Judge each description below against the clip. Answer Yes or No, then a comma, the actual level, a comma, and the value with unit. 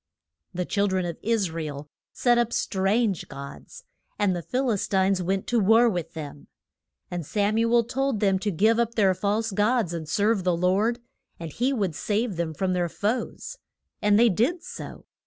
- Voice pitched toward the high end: Yes, high, 200 Hz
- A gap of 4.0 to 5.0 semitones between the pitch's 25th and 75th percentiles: Yes, average, 4.3 semitones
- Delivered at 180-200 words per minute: Yes, average, 195 wpm